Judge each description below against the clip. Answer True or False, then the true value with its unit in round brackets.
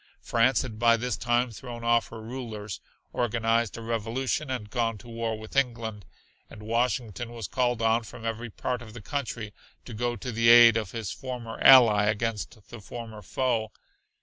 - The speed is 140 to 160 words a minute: False (175 wpm)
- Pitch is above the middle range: False (115 Hz)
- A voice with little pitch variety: True (1.7 semitones)